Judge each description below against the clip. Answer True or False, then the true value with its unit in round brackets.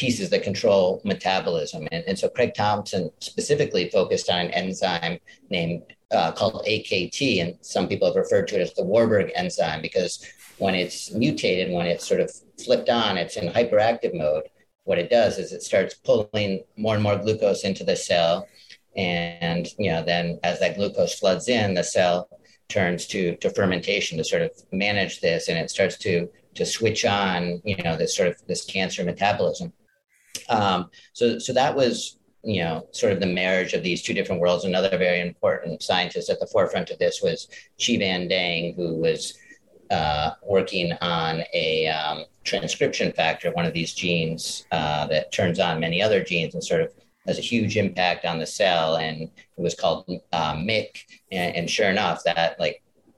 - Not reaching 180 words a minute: False (185 wpm)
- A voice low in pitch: True (105 Hz)